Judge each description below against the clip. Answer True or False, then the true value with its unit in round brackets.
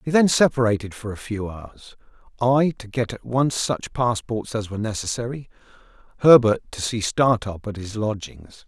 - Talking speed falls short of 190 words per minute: True (165 wpm)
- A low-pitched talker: True (115 Hz)